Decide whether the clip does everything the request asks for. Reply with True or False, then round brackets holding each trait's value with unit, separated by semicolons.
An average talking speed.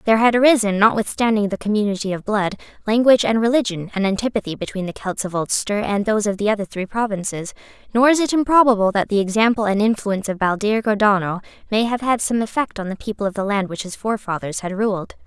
False (210 wpm)